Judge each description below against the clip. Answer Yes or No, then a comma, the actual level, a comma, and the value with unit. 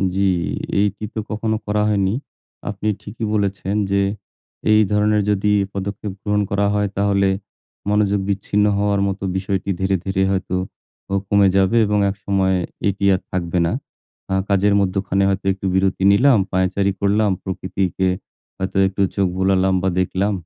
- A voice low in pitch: Yes, low, 100 Hz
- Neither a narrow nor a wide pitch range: No, narrow, 1.4 semitones